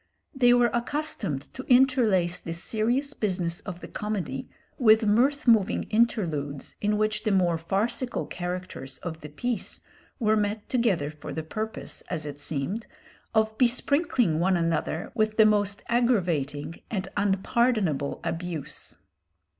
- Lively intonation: Yes, wide, 5.8 semitones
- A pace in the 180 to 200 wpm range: No, slow, 135 wpm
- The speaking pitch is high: Yes, high, 205 Hz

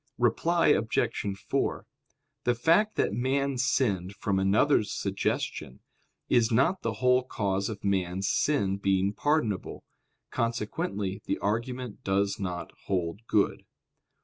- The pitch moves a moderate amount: Yes, average, 4.5 semitones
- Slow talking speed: Yes, slow, 120 wpm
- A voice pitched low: Yes, low, 110 Hz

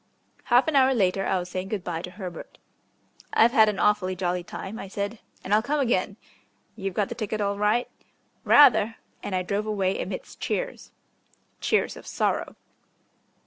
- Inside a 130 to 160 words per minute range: No, average, 175 wpm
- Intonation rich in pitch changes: No, average, 3.3 semitones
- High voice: Yes, high, 205 Hz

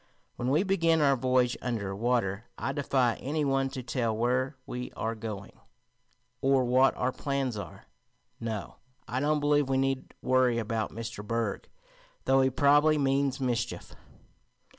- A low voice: Yes, low, 130 Hz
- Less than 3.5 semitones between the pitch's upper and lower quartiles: Yes, average, 2.9 semitones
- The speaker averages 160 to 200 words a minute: No, average, 150 wpm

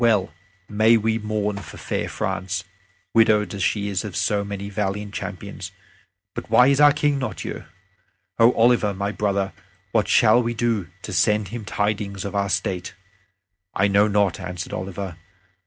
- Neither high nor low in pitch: No, low, 105 Hz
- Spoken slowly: No, average, 165 wpm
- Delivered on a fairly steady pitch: Yes, narrow, 2.1 semitones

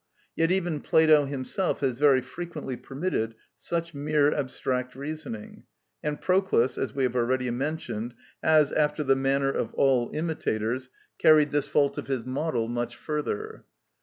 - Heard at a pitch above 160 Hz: No, medium, 140 Hz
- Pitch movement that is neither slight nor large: Yes, average, 3.3 semitones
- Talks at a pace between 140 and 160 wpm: Yes, average, 145 wpm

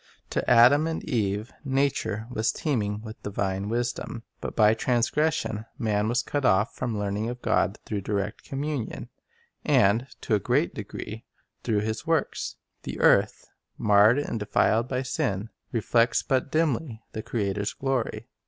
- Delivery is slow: No, average, 150 wpm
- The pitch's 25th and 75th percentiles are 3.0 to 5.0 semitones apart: Yes, average, 3.7 semitones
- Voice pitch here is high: No, low, 115 Hz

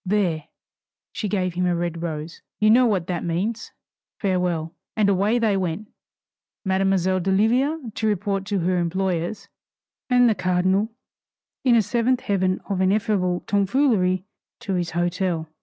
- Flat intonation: No, average, 3.1 semitones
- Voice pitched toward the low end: No, high, 190 Hz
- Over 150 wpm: No, average, 140 wpm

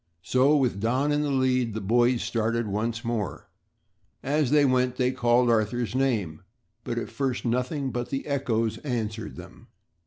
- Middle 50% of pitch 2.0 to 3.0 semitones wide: Yes, average, 2.7 semitones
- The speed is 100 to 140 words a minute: No, average, 160 wpm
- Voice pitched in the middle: No, low, 120 Hz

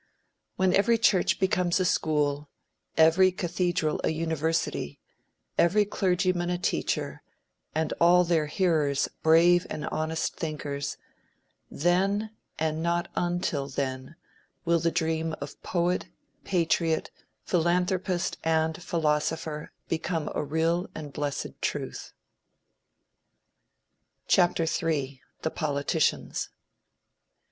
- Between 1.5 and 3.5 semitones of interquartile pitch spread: Yes, narrow, 2.4 semitones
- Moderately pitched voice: Yes, medium, 165 Hz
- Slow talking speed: Yes, slow, 100 wpm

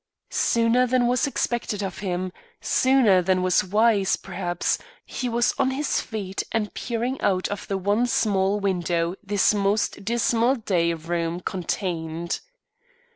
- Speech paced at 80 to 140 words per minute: Yes, slow, 135 wpm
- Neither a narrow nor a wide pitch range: Yes, average, 4.4 semitones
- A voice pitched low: No, high, 200 Hz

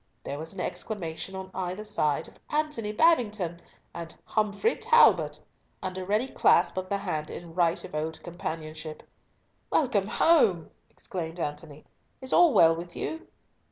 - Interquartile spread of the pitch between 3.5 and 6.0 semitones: Yes, average, 4.6 semitones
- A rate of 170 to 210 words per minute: No, average, 150 wpm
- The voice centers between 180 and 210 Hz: Yes, medium, 185 Hz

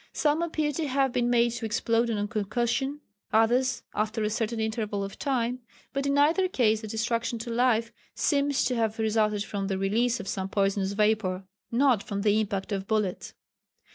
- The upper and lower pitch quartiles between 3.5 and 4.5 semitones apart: No, average, 3.0 semitones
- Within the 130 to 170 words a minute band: No, average, 180 wpm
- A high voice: Yes, high, 225 Hz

